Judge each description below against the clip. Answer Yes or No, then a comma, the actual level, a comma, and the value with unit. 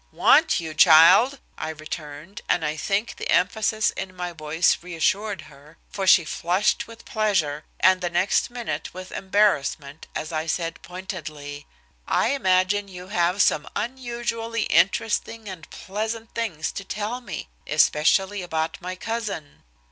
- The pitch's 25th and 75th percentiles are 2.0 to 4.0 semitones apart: No, average, 4.8 semitones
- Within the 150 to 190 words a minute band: No, average, 140 wpm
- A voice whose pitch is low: No, medium, 185 Hz